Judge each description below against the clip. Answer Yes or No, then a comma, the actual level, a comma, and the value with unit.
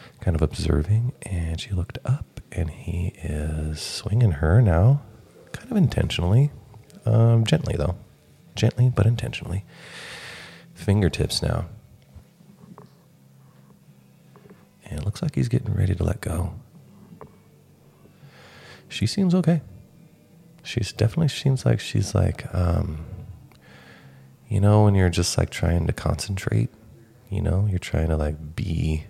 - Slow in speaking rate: Yes, slow, 125 wpm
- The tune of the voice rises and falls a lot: Yes, wide, 5.7 semitones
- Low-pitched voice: Yes, low, 100 Hz